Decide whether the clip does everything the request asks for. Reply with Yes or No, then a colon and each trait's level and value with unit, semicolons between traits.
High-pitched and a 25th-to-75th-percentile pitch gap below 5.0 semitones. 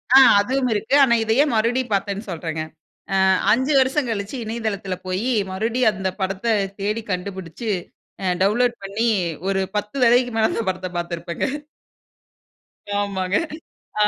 Yes: high, 210 Hz; average, 3.7 semitones